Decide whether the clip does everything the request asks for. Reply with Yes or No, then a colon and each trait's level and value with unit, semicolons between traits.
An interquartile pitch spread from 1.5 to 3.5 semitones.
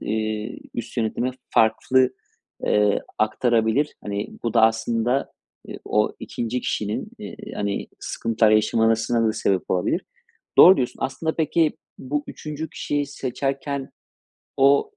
No: average, 3.9 semitones